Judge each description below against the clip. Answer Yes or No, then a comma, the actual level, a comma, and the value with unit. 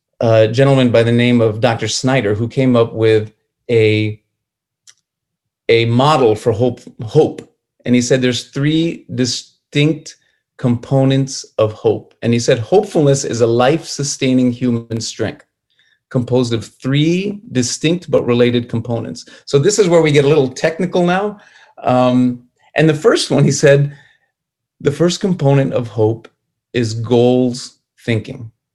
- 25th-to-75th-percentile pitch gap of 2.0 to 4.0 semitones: Yes, average, 3.6 semitones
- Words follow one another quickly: No, average, 145 wpm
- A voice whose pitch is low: Yes, low, 125 Hz